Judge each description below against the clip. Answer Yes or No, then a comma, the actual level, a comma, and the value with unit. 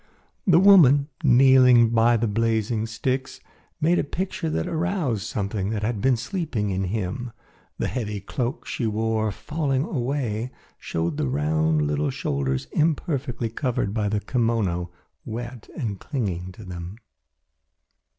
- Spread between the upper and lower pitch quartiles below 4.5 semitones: No, average, 4.9 semitones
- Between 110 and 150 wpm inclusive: Yes, slow, 135 wpm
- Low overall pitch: Yes, low, 115 Hz